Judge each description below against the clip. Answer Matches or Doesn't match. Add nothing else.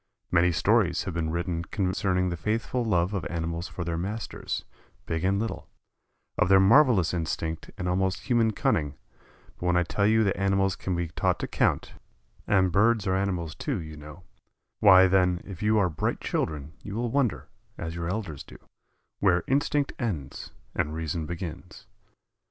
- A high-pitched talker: Doesn't match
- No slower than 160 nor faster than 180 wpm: Matches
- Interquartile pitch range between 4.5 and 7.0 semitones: Doesn't match